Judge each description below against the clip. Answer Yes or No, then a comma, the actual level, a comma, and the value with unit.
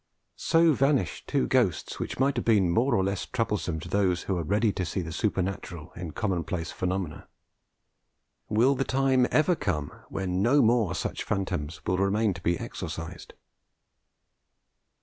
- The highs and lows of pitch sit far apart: Yes, wide, 5.7 semitones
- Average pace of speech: Yes, average, 155 wpm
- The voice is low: Yes, very low, 95 Hz